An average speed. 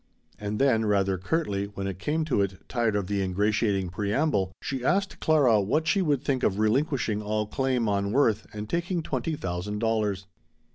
Yes: average, 180 wpm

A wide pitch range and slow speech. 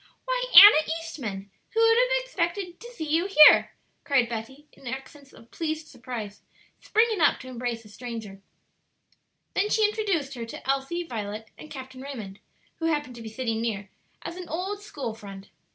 No: wide, 7.4 semitones; average, 170 wpm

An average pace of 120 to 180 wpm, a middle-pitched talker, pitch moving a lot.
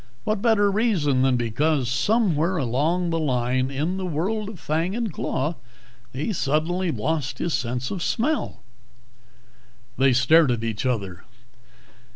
Yes: average, 140 wpm; medium, 155 Hz; wide, 6.4 semitones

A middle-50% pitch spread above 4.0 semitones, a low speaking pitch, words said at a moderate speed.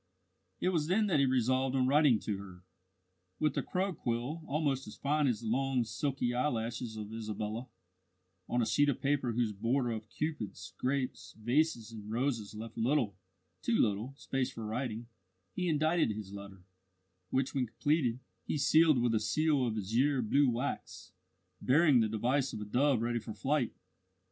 Yes: average, 4.5 semitones; low, 125 Hz; average, 170 wpm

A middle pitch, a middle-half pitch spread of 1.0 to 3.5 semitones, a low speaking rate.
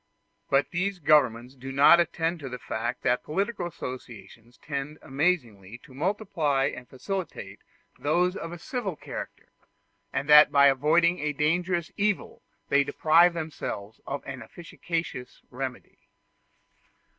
No: medium, 150 Hz; average, 4.8 semitones; slow, 130 wpm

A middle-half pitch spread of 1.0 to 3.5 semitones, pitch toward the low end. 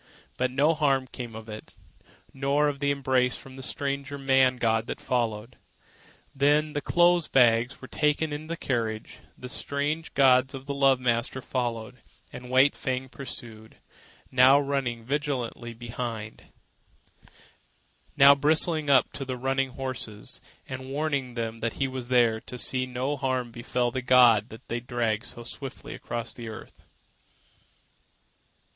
Yes: average, 2.8 semitones; low, 130 Hz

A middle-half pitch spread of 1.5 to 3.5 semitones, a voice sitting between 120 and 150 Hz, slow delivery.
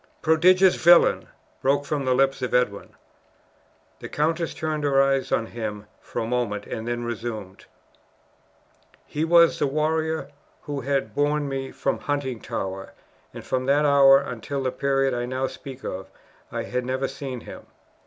No: average, 3.2 semitones; low, 135 Hz; average, 155 wpm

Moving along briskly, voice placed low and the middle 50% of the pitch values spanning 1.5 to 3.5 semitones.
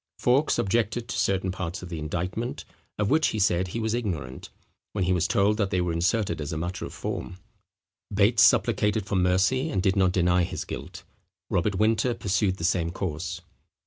No: average, 190 wpm; very low, 95 Hz; average, 3.2 semitones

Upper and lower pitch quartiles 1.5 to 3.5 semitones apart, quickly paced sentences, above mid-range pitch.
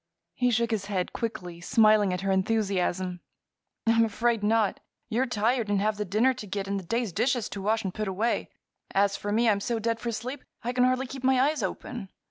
Yes: average, 3.2 semitones; fast, 215 wpm; high, 215 Hz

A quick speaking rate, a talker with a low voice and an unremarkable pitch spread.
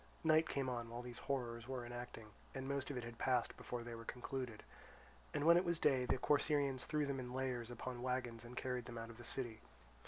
No: fast, 220 wpm; low, 125 Hz; narrow, 2.3 semitones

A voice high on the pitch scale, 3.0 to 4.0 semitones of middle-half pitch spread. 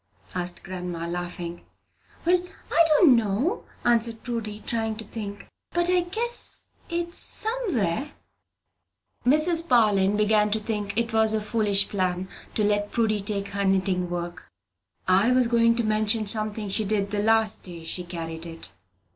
Yes: high, 215 Hz; average, 3.5 semitones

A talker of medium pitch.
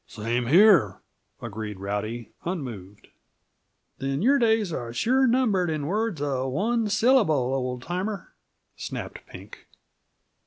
Yes: medium, 150 Hz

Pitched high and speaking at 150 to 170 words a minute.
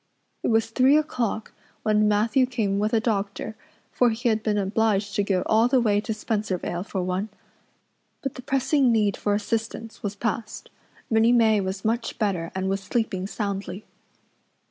Yes: high, 215 Hz; average, 165 wpm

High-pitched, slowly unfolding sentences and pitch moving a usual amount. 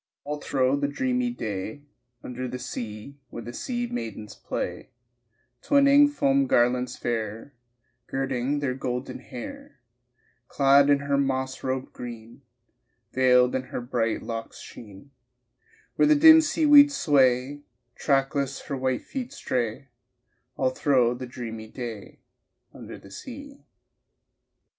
No: low, 130 Hz; slow, 125 wpm; average, 3.5 semitones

